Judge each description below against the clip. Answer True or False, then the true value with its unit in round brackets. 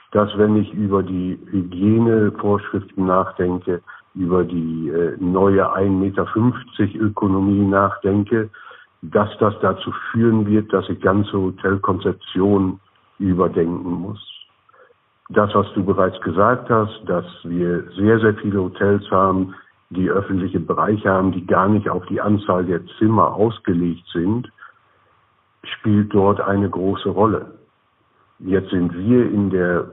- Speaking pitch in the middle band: False (100 Hz)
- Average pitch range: False (2.2 semitones)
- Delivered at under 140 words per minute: True (125 wpm)